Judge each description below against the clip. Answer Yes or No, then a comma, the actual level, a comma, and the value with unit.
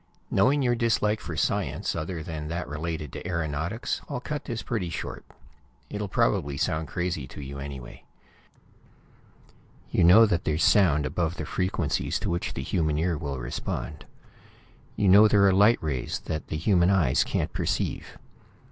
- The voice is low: Yes, very low, 85 Hz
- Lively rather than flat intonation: No, average, 4.9 semitones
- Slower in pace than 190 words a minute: Yes, average, 160 wpm